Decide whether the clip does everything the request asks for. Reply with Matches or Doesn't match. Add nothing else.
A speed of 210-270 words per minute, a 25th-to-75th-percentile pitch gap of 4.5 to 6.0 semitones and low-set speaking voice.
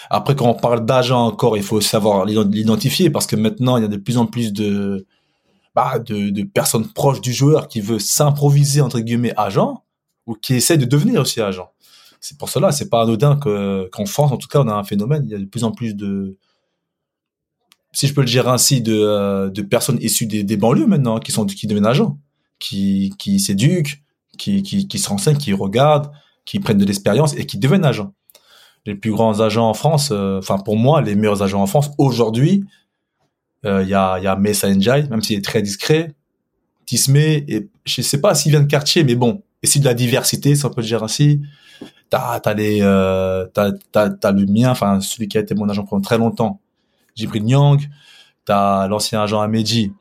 Matches